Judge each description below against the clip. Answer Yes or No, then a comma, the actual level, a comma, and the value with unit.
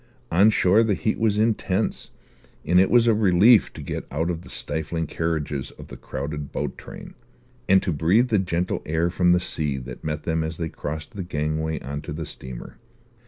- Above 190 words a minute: Yes, average, 200 wpm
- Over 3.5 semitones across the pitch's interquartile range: Yes, average, 3.9 semitones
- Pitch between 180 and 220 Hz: No, very low, 85 Hz